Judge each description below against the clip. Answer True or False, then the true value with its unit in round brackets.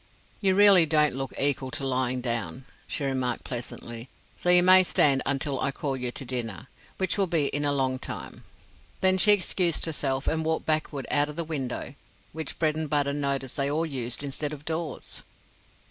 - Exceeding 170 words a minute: True (180 wpm)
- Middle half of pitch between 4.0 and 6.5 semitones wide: False (3.3 semitones)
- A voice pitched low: False (145 Hz)